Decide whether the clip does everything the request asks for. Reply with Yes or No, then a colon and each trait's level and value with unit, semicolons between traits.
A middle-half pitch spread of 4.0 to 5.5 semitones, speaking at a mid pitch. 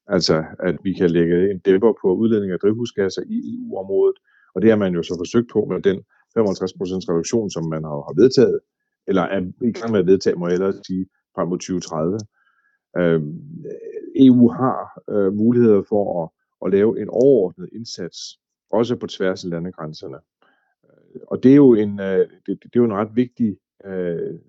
No: average, 4.8 semitones; low, 100 Hz